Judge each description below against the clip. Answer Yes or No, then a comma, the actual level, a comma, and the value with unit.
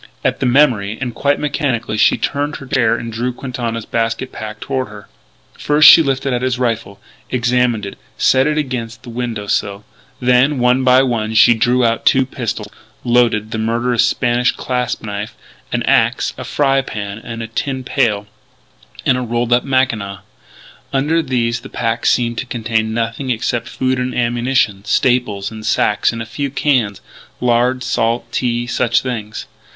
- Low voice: Yes, low, 120 Hz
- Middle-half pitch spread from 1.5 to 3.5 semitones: Yes, narrow, 2.4 semitones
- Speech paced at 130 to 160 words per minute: No, average, 170 wpm